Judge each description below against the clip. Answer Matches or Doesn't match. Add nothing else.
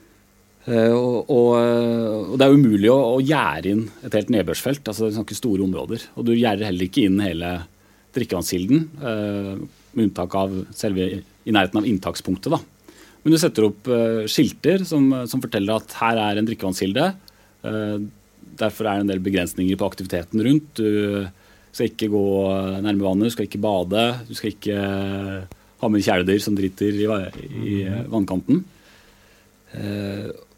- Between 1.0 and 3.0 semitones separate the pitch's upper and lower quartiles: Matches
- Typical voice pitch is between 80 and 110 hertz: Matches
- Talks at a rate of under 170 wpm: Matches